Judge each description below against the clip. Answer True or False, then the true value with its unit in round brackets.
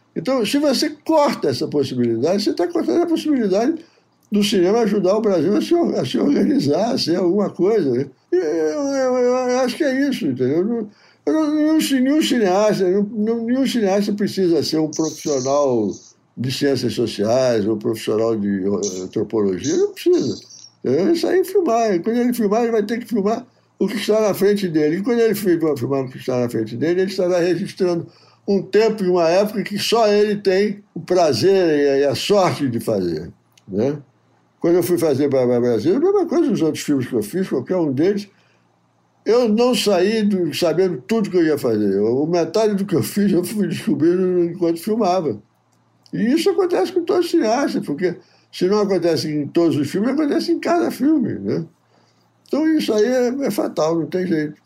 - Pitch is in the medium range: False (195 Hz)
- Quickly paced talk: True (190 wpm)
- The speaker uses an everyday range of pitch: False (7.6 semitones)